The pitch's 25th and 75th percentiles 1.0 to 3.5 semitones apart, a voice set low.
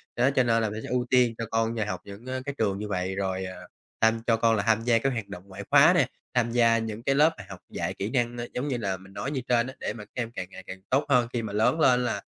Yes: average, 3.2 semitones; low, 115 Hz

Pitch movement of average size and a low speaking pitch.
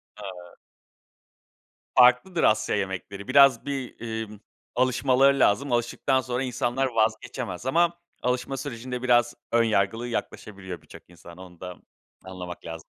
Yes: average, 4.9 semitones; low, 120 Hz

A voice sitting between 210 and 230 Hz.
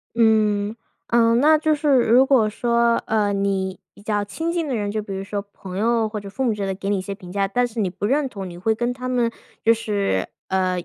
Yes: high, 215 Hz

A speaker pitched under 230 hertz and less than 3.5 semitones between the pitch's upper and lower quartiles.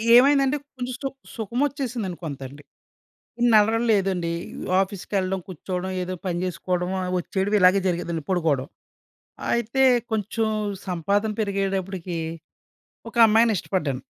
No: high, 190 Hz; average, 3.9 semitones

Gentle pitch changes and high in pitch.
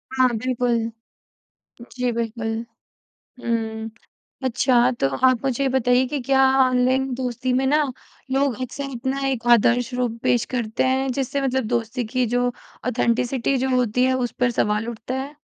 Yes: narrow, 1.9 semitones; very high, 250 Hz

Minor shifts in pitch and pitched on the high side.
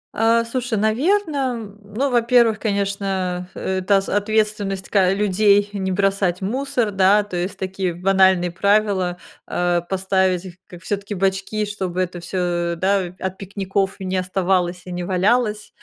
Yes: narrow, 2.3 semitones; high, 195 Hz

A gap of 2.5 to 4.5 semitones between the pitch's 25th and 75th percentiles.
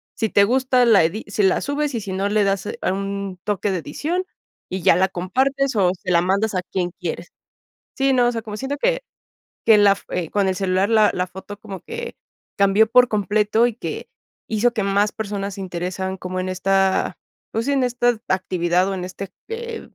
Yes: average, 3.9 semitones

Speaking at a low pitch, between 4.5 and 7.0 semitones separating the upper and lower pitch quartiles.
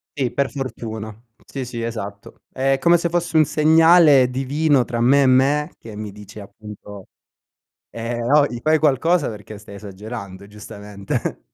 Yes: low, 120 Hz; wide, 5.6 semitones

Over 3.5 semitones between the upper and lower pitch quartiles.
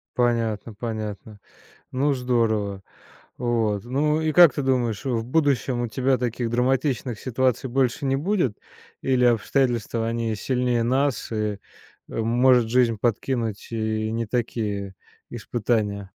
No: average, 2.9 semitones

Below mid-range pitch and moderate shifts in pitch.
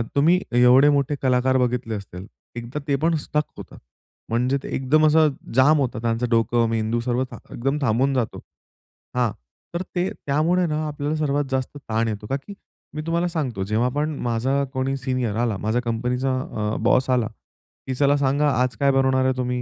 Yes: low, 130 Hz; average, 3.5 semitones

